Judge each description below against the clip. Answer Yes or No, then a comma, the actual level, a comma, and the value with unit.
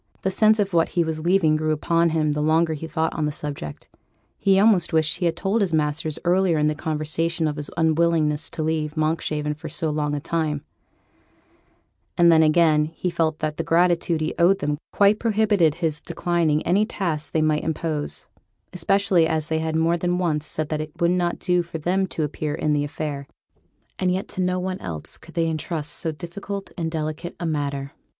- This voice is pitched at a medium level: Yes, medium, 160 Hz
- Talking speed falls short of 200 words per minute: No, fast, 205 wpm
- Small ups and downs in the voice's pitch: Yes, narrow, 2.3 semitones